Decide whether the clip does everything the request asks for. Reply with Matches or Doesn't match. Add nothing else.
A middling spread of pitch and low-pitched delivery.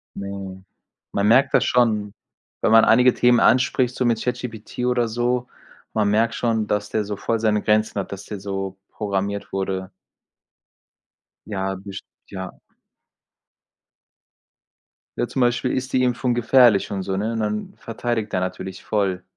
Matches